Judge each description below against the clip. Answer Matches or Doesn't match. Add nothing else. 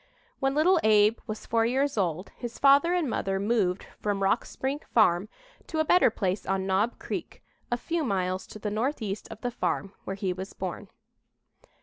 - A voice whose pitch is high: Matches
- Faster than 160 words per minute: Matches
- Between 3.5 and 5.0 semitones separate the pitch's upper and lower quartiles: Doesn't match